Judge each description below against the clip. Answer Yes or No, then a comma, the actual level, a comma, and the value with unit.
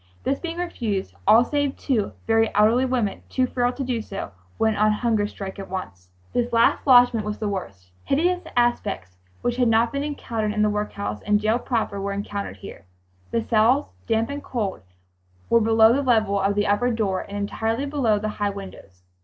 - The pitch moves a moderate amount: Yes, average, 3.3 semitones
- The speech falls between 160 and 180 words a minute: No, average, 190 wpm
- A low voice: No, high, 220 Hz